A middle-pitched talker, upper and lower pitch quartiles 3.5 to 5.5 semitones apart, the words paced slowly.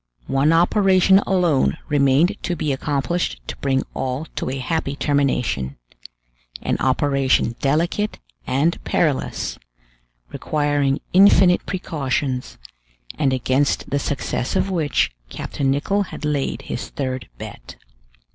Yes: medium, 145 Hz; average, 4.1 semitones; slow, 115 wpm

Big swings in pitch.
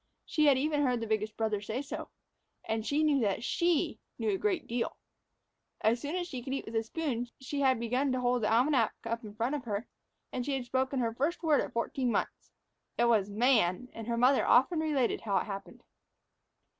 No: average, 3.8 semitones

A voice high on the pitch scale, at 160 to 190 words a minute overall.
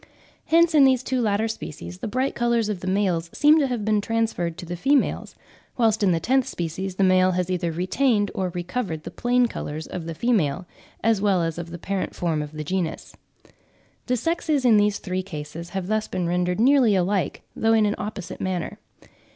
No: high, 195 Hz; average, 200 wpm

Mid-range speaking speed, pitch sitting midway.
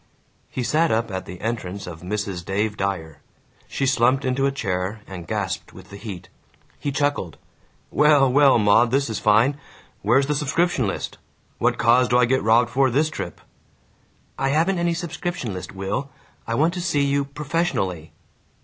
No: average, 170 wpm; low, 120 Hz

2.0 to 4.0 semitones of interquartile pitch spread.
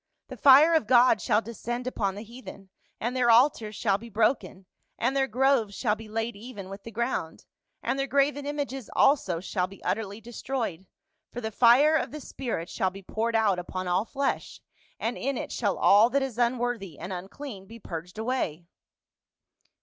No: average, 4.6 semitones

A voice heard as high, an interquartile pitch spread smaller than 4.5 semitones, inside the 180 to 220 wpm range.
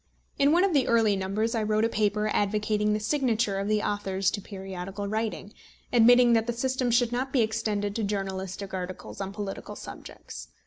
Yes: high, 215 Hz; average, 2.8 semitones; average, 185 wpm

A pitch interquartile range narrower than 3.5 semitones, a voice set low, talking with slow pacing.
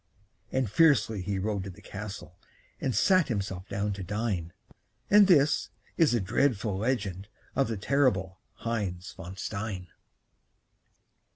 No: average, 4.9 semitones; low, 105 Hz; slow, 130 wpm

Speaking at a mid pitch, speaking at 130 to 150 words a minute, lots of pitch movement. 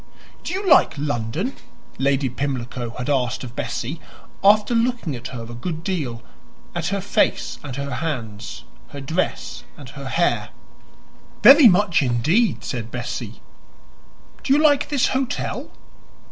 Yes: medium, 145 Hz; average, 140 wpm; wide, 9.0 semitones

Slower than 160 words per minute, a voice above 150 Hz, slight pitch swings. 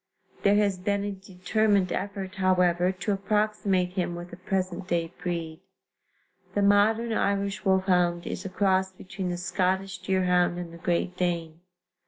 Yes: average, 150 wpm; medium, 185 Hz; narrow, 2.0 semitones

